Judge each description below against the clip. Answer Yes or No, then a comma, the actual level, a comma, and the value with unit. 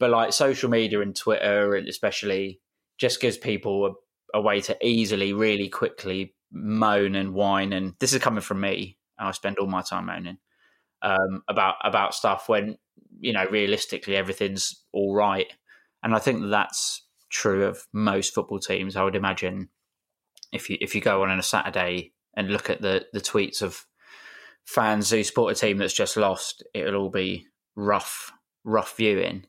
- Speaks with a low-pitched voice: Yes, low, 100 Hz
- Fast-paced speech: No, average, 175 wpm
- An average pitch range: No, narrow, 1.8 semitones